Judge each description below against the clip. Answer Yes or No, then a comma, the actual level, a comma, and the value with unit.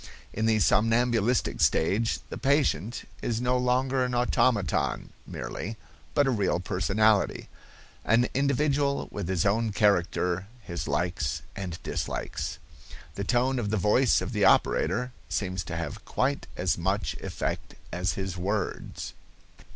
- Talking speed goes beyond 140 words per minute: No, slow, 135 wpm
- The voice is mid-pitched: No, low, 110 Hz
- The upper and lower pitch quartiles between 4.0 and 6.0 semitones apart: Yes, average, 5.0 semitones